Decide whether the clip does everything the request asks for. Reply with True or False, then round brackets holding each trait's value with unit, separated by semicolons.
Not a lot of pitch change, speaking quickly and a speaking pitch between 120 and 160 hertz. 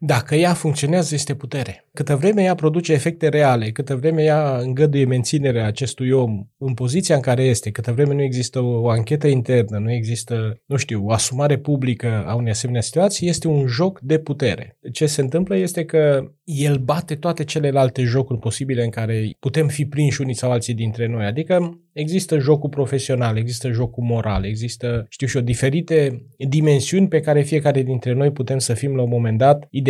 False (3.9 semitones; 185 wpm; 135 Hz)